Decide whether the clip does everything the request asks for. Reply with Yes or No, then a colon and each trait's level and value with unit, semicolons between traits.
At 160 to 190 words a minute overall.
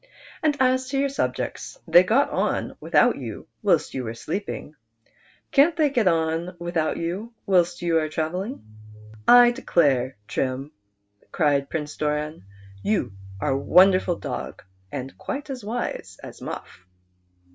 No: average, 145 wpm